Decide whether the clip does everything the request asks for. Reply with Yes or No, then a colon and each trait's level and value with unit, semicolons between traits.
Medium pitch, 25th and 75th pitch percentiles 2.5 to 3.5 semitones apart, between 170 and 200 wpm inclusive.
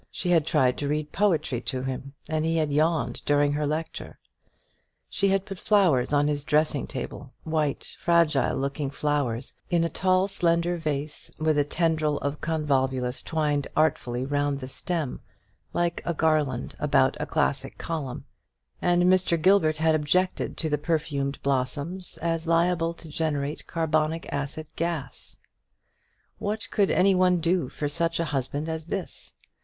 No: medium, 155 Hz; average, 2.8 semitones; average, 155 wpm